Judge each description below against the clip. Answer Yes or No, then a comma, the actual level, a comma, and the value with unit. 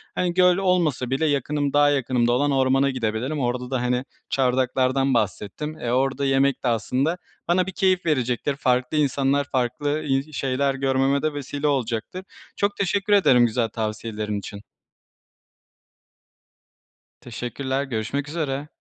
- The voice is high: No, low, 135 Hz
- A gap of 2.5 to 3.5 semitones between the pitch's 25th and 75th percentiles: Yes, average, 2.9 semitones